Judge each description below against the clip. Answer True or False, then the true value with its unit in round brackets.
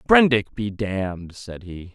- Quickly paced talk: False (155 wpm)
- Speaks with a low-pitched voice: True (105 Hz)